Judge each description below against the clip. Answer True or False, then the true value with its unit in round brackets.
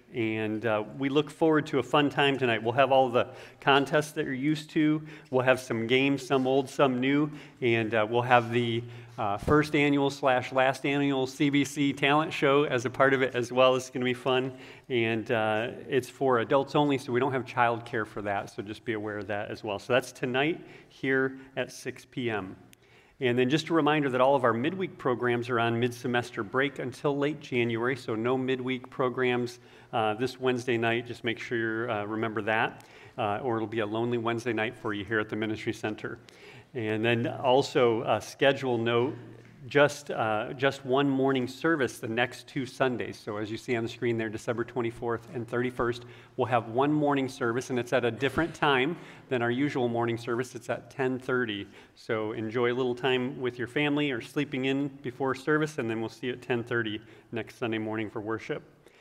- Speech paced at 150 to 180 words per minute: False (205 wpm)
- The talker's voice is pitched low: True (125 Hz)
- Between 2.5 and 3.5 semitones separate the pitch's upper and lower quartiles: True (2.8 semitones)